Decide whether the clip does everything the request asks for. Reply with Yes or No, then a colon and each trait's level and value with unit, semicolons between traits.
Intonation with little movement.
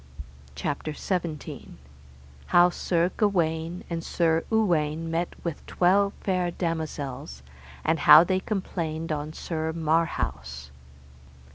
Yes: narrow, 2.3 semitones